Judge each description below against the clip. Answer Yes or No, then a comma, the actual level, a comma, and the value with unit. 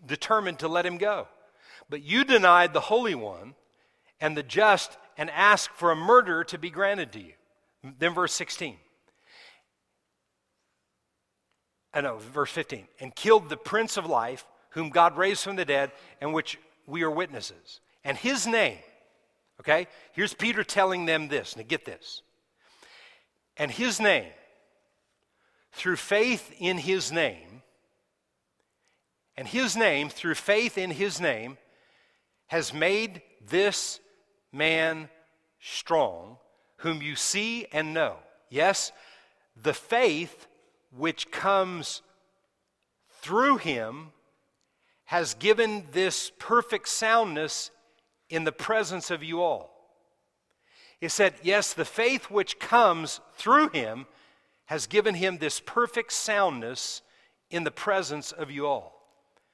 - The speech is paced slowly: Yes, slow, 125 wpm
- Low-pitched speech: No, medium, 180 Hz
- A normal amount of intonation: Yes, average, 5.0 semitones